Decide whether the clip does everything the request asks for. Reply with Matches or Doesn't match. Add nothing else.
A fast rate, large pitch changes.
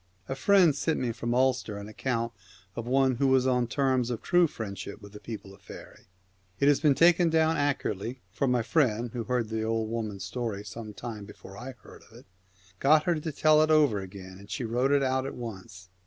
Doesn't match